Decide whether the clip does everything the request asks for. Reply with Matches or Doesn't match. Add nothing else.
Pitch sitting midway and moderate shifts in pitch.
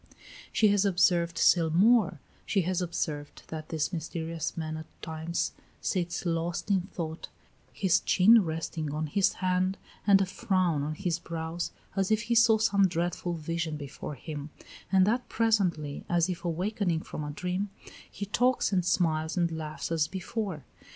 Matches